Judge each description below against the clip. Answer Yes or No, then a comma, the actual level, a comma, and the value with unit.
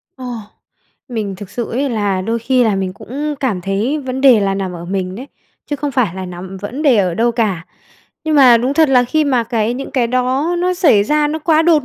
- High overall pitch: Yes, high, 240 Hz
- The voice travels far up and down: Yes, wide, 5.9 semitones